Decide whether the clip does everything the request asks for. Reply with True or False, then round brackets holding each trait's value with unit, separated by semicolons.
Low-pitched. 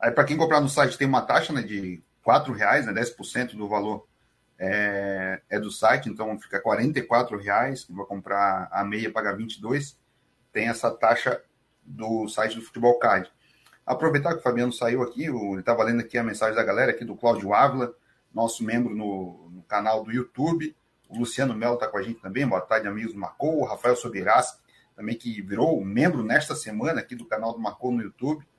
True (115 Hz)